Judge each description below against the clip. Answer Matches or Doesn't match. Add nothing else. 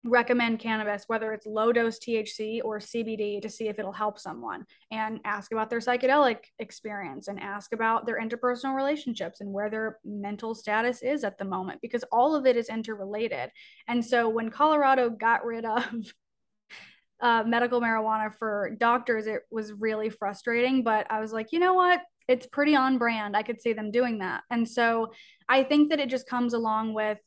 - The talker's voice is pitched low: Doesn't match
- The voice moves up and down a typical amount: Doesn't match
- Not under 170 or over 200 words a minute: Matches